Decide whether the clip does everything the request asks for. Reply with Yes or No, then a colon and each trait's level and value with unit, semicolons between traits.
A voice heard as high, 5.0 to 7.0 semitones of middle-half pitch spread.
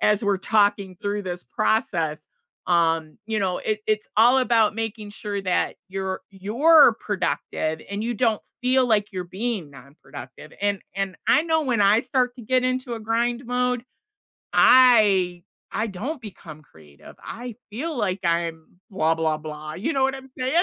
Yes: high, 205 Hz; wide, 5.5 semitones